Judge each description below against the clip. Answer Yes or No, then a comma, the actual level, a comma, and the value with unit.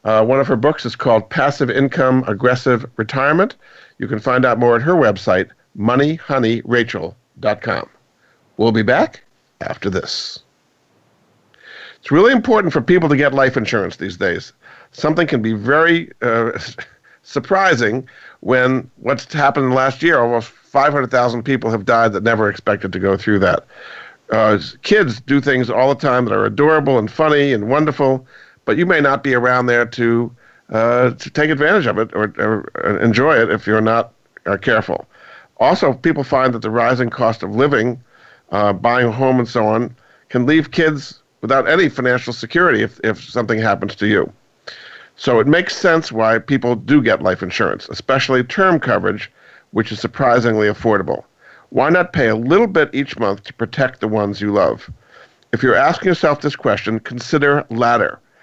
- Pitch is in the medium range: No, low, 125 Hz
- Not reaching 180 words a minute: Yes, average, 170 wpm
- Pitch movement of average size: Yes, average, 3.7 semitones